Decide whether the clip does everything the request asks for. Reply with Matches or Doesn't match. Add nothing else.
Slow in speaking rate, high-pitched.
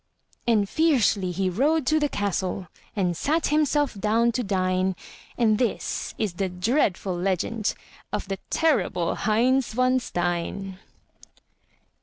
Matches